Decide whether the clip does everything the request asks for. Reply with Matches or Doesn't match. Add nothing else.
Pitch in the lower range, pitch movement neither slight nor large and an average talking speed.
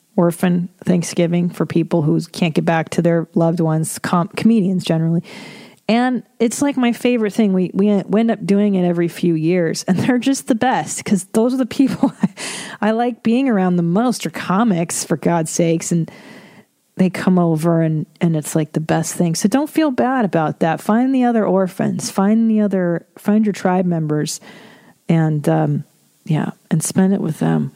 Doesn't match